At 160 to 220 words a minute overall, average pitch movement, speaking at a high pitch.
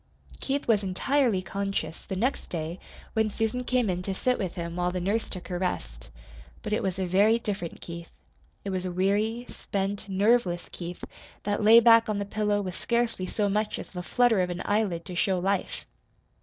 Yes: average, 195 wpm; average, 3.5 semitones; high, 195 Hz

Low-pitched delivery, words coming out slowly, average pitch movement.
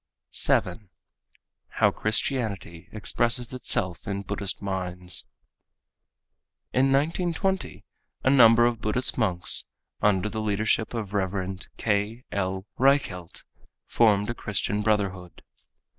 Yes: low, 105 Hz; slow, 100 wpm; average, 3.9 semitones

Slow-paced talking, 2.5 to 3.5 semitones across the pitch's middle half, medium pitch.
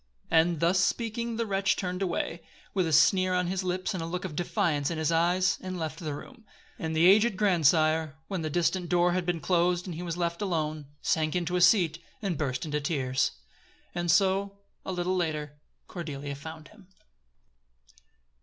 No: average, 185 wpm; average, 2.8 semitones; medium, 175 Hz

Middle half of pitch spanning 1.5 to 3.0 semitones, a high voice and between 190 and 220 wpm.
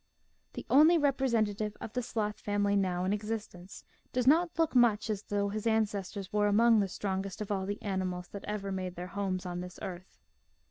Yes: narrow, 2.6 semitones; high, 205 Hz; average, 195 wpm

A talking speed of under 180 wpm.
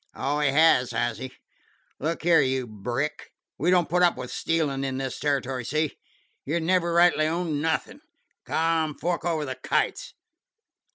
Yes: average, 160 wpm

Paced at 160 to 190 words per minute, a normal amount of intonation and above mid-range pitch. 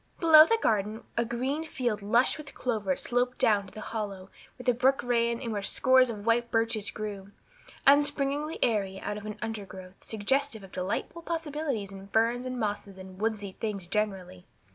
Yes: average, 175 wpm; average, 4.1 semitones; high, 225 Hz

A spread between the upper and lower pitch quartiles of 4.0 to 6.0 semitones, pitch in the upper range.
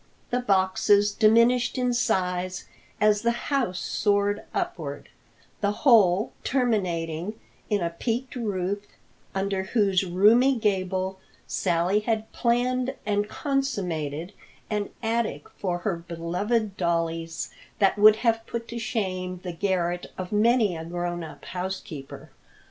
Yes: average, 4.4 semitones; high, 205 Hz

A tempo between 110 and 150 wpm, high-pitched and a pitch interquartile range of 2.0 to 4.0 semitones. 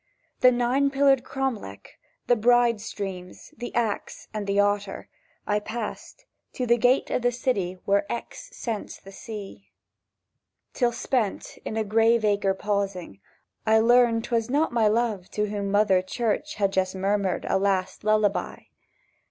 Yes: average, 145 wpm; high, 215 Hz; average, 3.3 semitones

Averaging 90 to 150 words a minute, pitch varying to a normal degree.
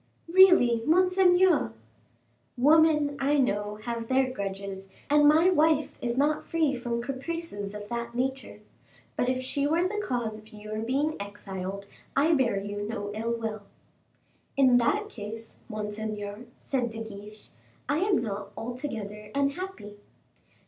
No: average, 140 wpm; wide, 6.0 semitones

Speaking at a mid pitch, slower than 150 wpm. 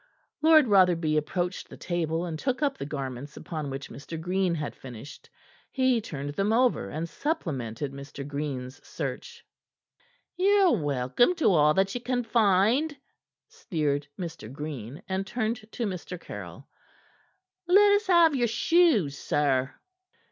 Yes: medium, 180 Hz; average, 140 wpm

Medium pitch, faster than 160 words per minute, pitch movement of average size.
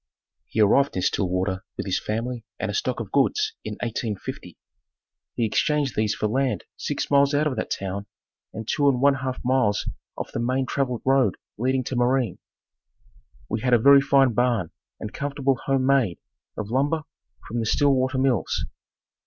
No: low, 125 Hz; average, 170 wpm; average, 3.9 semitones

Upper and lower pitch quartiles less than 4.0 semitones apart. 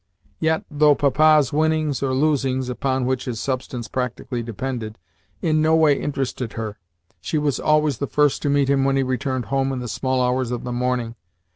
Yes: average, 2.8 semitones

